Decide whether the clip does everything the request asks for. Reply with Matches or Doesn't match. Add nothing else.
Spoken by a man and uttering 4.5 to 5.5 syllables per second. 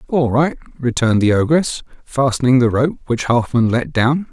Matches